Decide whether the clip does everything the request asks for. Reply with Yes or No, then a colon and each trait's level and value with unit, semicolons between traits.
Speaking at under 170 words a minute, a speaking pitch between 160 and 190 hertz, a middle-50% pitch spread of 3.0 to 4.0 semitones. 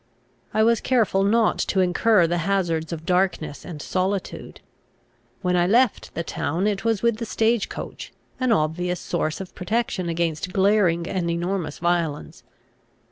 Yes: average, 150 wpm; medium, 185 Hz; average, 3.7 semitones